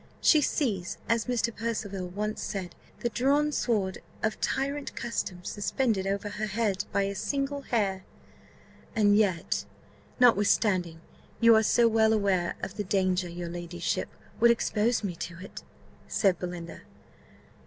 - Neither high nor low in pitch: No, high, 205 Hz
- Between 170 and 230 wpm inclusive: No, average, 140 wpm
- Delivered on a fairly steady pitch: No, average, 3.9 semitones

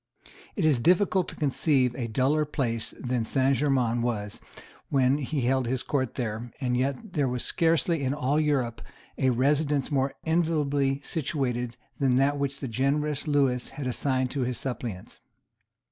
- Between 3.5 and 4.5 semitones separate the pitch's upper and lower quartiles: No, average, 2.9 semitones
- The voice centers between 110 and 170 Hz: Yes, low, 135 Hz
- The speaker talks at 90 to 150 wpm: No, average, 160 wpm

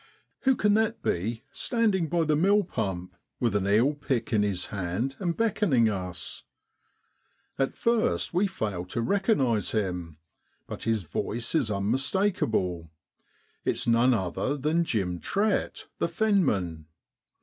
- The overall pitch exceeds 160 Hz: No, low, 120 Hz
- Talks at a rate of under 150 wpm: Yes, average, 140 wpm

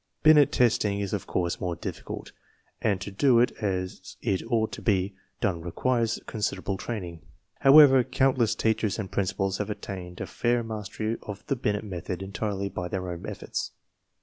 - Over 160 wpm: Yes, average, 170 wpm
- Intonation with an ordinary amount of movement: Yes, average, 3.6 semitones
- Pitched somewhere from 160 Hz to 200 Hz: No, low, 105 Hz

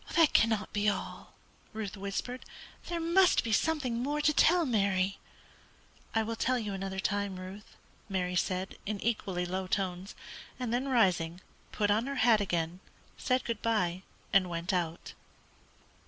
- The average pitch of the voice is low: No, high, 205 Hz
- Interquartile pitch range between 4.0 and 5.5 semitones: Yes, average, 4.5 semitones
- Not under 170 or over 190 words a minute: No, average, 155 wpm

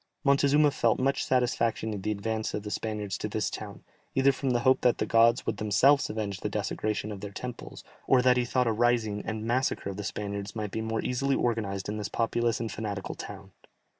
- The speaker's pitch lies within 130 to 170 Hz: No, low, 110 Hz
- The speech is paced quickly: Yes, fast, 215 wpm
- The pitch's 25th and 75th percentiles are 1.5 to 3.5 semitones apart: Yes, average, 3.1 semitones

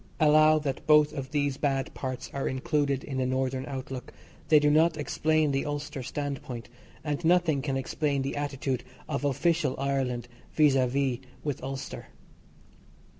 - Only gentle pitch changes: Yes, narrow, 2.2 semitones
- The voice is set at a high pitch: No, medium, 140 Hz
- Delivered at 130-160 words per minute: Yes, average, 155 wpm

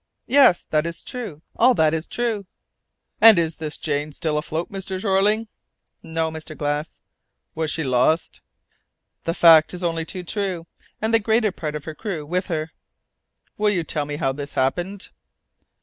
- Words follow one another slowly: No, average, 165 wpm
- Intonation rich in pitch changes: No, average, 4.3 semitones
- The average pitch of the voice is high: No, medium, 165 Hz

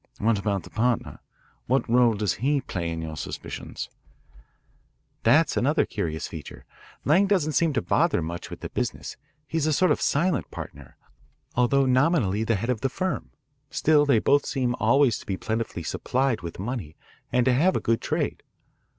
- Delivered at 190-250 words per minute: No, average, 175 wpm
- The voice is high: No, low, 125 Hz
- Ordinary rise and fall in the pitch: No, wide, 6.0 semitones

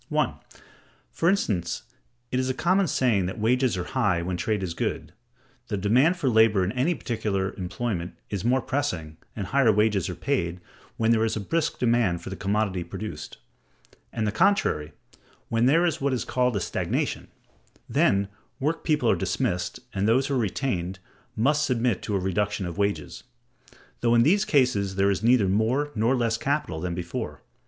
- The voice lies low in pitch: Yes, low, 110 Hz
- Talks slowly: No, average, 180 wpm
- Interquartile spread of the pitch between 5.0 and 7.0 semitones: Yes, average, 5.3 semitones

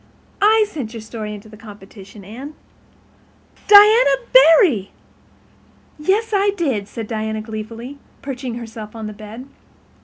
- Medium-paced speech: No, slow, 120 wpm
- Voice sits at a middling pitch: No, high, 230 Hz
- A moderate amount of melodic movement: No, wide, 7.4 semitones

